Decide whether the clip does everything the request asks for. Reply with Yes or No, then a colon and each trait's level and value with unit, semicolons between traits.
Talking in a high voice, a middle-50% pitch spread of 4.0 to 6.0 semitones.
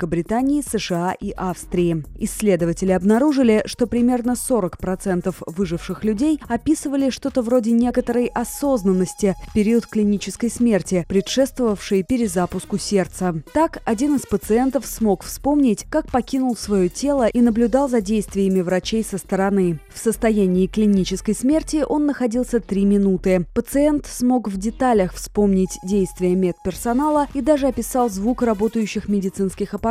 Yes: high, 215 Hz; average, 4.7 semitones